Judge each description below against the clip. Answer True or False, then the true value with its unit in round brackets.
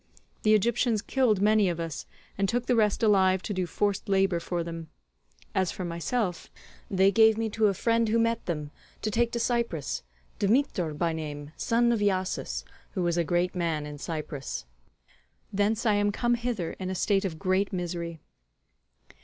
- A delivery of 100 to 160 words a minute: False (180 wpm)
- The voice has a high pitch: True (195 Hz)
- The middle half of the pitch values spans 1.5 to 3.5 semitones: False (4.5 semitones)